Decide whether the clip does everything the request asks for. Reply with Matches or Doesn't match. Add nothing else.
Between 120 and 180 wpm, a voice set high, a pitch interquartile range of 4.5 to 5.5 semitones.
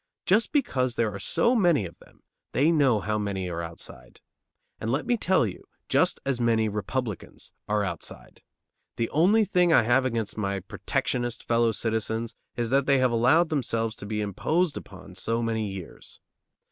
Doesn't match